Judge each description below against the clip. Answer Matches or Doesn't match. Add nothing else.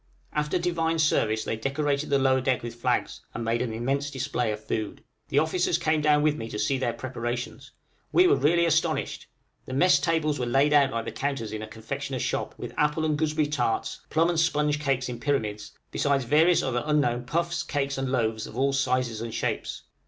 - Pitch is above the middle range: Doesn't match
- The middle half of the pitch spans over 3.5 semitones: Matches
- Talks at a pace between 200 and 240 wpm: Matches